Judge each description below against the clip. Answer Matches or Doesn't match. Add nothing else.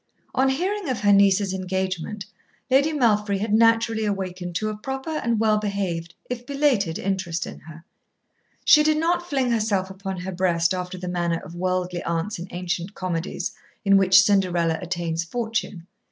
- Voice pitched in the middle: Doesn't match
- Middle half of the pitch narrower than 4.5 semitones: Matches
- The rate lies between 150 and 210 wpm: Matches